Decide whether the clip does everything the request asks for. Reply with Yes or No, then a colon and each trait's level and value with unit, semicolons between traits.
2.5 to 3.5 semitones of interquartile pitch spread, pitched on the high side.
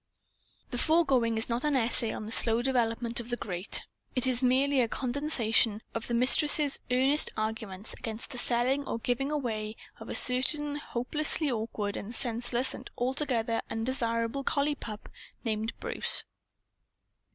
Yes: average, 3.0 semitones; high, 240 Hz